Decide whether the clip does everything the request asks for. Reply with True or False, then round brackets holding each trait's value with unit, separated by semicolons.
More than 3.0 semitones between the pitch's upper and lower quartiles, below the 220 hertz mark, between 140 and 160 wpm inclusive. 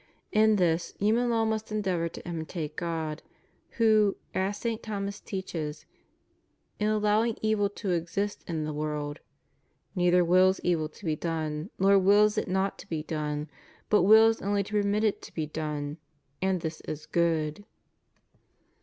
True (4.7 semitones; 185 Hz; 155 wpm)